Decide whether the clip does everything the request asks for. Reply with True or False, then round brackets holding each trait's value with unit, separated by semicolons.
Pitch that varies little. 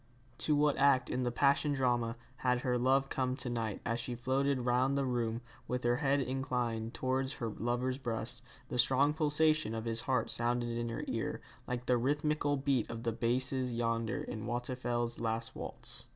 True (2.3 semitones)